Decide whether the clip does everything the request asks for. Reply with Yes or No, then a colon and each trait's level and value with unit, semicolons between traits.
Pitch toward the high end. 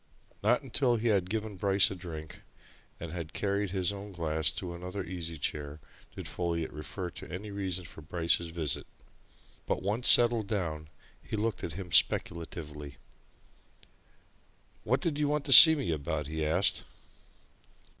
No: very low, 90 Hz